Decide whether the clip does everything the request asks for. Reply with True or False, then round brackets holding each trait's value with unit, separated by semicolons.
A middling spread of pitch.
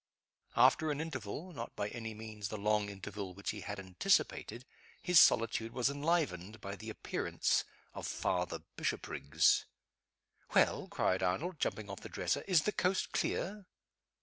False (7.2 semitones)